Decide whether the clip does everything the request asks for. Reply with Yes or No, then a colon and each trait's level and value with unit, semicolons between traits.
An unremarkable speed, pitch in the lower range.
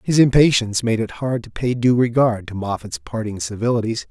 Yes: average, 190 wpm; low, 115 Hz